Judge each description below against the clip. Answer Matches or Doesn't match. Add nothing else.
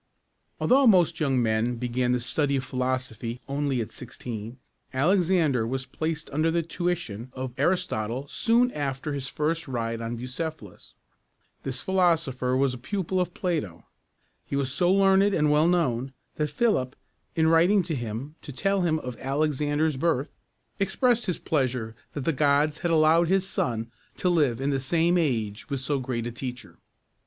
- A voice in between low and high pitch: Matches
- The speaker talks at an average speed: Matches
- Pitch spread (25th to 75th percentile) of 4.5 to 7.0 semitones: Matches